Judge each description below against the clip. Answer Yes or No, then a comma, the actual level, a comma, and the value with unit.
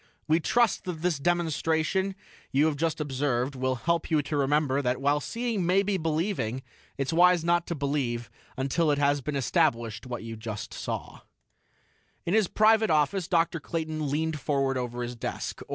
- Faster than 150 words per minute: Yes, average, 170 wpm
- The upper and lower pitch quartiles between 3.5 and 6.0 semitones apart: Yes, average, 4.1 semitones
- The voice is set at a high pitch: No, medium, 150 Hz